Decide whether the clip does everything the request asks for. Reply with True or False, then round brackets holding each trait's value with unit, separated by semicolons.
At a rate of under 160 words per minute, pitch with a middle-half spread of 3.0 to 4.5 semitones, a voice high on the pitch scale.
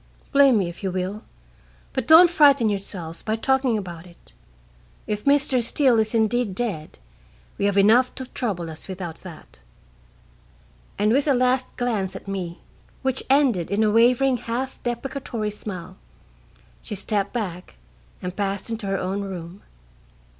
False (150 wpm; 4.9 semitones; 215 Hz)